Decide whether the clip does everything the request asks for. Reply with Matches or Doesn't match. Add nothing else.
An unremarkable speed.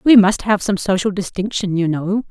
Doesn't match